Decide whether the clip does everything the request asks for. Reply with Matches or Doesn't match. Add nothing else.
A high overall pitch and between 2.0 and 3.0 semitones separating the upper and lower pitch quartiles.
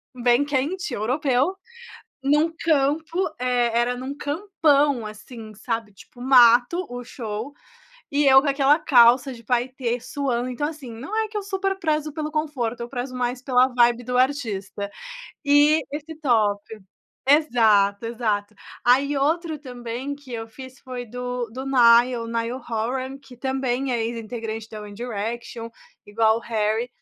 Doesn't match